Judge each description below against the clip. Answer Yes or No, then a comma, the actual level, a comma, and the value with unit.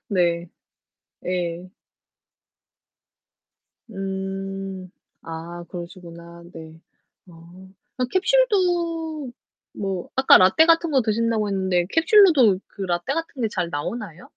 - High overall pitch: Yes, high, 195 Hz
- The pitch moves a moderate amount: No, wide, 7.3 semitones